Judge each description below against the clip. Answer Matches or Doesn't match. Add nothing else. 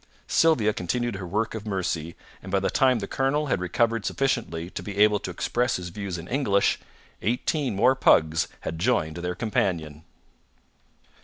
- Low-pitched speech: Matches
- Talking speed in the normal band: Matches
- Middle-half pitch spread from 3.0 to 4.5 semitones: Doesn't match